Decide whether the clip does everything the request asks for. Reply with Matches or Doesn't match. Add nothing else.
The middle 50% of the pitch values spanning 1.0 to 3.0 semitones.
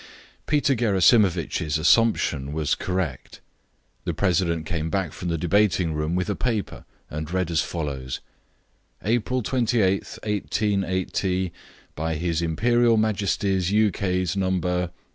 Doesn't match